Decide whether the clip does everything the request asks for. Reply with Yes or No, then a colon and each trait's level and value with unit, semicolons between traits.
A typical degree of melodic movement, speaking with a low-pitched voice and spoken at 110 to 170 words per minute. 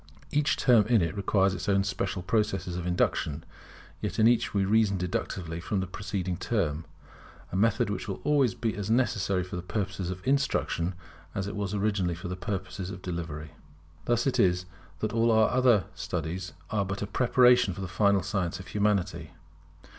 No: average, 3.2 semitones; low, 100 Hz; average, 180 wpm